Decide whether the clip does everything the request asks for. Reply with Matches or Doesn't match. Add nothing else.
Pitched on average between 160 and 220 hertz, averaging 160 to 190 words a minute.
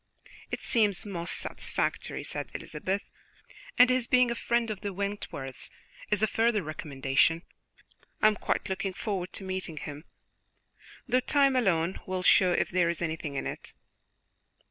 Doesn't match